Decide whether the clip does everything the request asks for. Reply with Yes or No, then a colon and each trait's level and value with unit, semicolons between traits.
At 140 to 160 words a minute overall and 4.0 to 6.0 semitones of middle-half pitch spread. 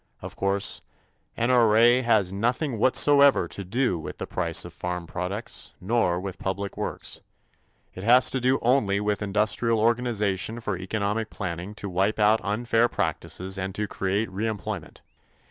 No: average, 145 wpm; average, 3.4 semitones